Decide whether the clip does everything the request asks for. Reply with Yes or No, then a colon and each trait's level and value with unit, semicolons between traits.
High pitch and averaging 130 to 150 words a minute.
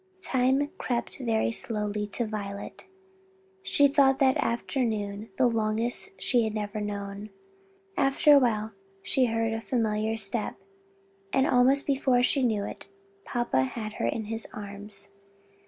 Yes: high, 225 Hz; average, 140 wpm